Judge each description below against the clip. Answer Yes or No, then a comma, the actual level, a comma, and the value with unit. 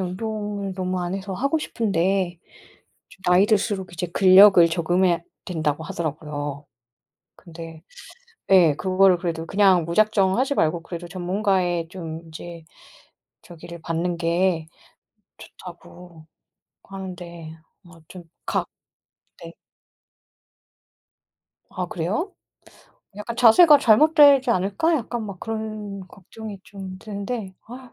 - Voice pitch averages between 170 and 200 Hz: Yes, medium, 185 Hz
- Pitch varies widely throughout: No, average, 3.4 semitones